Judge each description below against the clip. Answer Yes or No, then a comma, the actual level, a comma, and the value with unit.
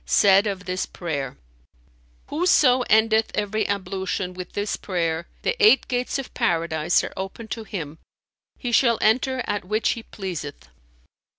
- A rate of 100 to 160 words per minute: Yes, average, 140 wpm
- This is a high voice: Yes, high, 200 Hz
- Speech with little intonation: No, average, 4.2 semitones